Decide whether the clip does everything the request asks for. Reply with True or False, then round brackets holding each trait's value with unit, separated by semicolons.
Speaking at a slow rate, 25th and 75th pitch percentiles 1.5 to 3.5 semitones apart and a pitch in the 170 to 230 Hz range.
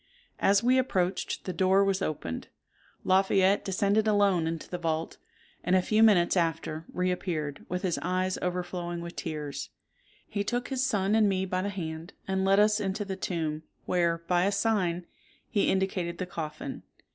False (170 wpm; 2.6 semitones; 185 Hz)